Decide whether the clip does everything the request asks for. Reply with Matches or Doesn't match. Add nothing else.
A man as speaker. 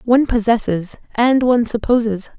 Doesn't match